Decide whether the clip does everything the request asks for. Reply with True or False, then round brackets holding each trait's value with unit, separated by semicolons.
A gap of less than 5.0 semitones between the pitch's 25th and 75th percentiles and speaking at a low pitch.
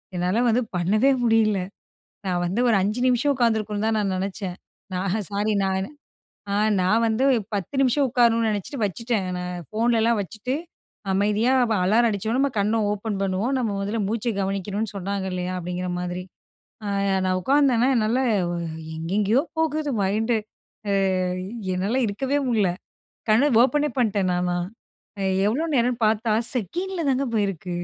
False (3.8 semitones; 215 Hz)